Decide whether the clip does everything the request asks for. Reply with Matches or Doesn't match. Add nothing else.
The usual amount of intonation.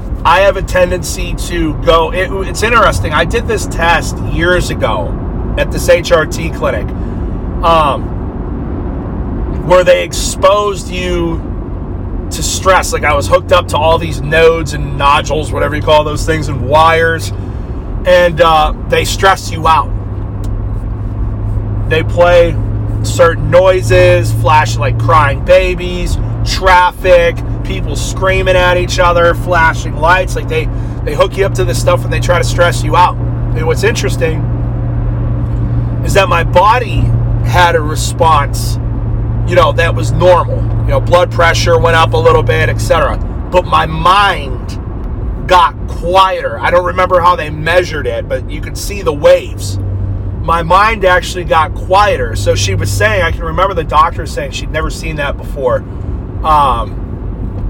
Doesn't match